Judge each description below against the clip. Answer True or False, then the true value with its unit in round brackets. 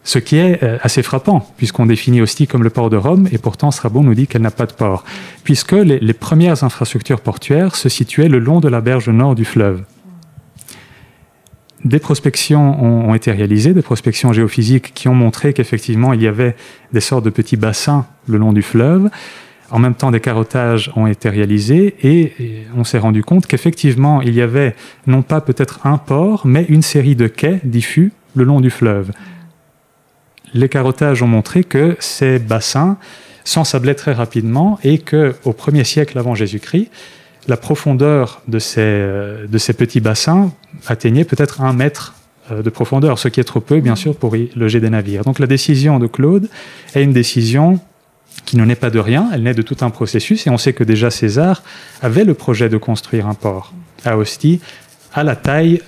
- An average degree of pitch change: True (4.3 semitones)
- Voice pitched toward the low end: True (130 Hz)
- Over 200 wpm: False (190 wpm)